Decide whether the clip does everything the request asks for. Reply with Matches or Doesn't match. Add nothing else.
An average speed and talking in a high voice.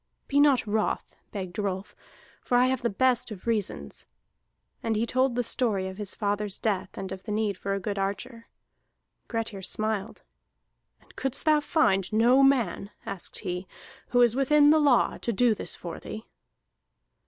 Matches